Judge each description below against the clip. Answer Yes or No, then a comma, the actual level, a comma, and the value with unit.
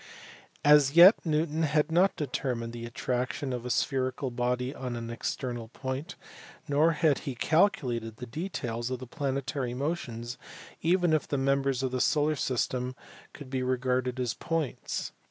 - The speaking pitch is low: Yes, low, 130 Hz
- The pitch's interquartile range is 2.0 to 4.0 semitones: Yes, average, 3.3 semitones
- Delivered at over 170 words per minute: No, average, 160 wpm